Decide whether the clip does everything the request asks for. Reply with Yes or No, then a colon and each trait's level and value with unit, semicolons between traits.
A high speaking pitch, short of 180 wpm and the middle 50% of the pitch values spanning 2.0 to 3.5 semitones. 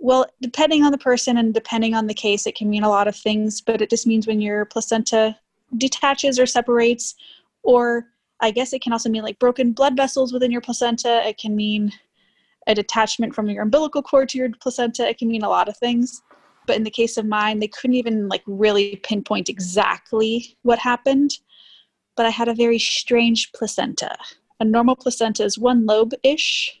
No: high, 230 Hz; average, 195 wpm; narrow, 2.5 semitones